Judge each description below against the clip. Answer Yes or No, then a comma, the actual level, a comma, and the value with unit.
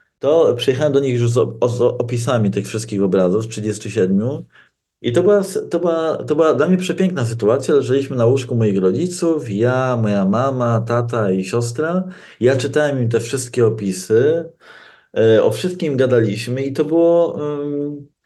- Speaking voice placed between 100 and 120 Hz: No, low, 135 Hz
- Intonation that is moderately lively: No, wide, 6.1 semitones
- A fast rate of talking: Yes, fast, 165 wpm